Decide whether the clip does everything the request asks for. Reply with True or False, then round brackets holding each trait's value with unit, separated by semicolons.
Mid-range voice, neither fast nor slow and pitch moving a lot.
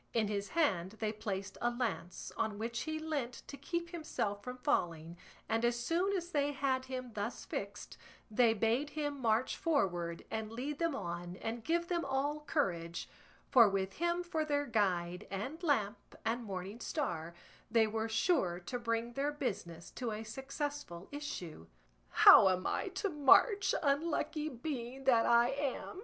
False (240 Hz; 165 wpm; 6.3 semitones)